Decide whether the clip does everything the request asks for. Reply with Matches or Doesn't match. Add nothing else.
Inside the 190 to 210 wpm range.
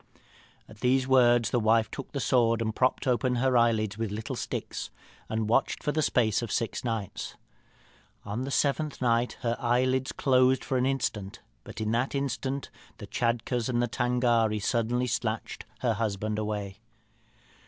Doesn't match